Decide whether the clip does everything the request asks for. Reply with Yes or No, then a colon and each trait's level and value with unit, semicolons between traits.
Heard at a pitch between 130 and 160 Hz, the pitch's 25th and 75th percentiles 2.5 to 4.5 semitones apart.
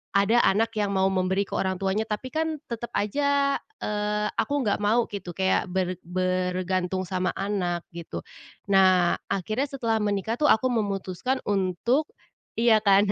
No: high, 200 Hz; average, 3.4 semitones